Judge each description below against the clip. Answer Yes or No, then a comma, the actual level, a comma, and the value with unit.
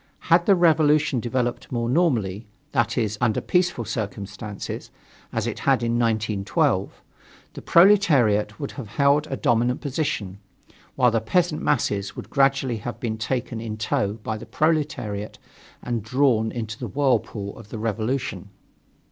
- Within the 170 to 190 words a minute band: No, average, 150 wpm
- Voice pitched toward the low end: Yes, low, 120 Hz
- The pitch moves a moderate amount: Yes, average, 4.5 semitones